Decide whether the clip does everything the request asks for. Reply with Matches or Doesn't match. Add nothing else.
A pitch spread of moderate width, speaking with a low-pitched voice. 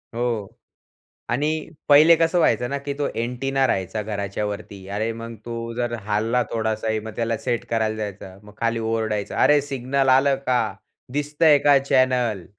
Matches